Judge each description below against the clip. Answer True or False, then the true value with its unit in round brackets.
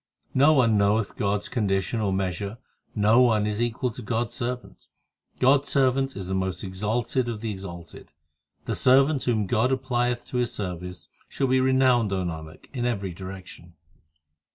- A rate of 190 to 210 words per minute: False (175 wpm)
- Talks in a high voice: False (110 Hz)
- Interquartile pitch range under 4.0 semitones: False (4.6 semitones)